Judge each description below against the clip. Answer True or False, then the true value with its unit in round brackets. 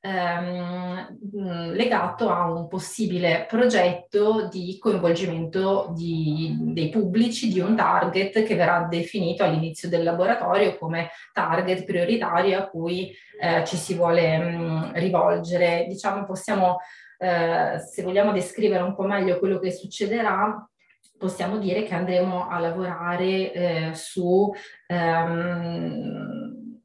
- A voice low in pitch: False (180 Hz)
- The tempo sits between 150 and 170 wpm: False (115 wpm)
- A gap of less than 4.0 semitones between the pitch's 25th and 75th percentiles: True (2.7 semitones)